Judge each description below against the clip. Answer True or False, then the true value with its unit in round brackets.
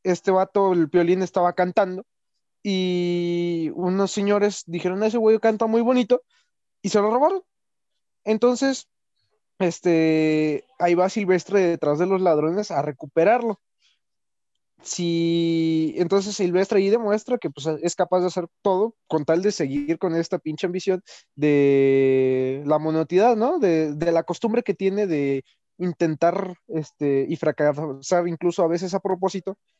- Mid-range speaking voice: True (180 Hz)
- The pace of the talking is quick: False (140 wpm)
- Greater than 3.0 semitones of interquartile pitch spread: True (3.8 semitones)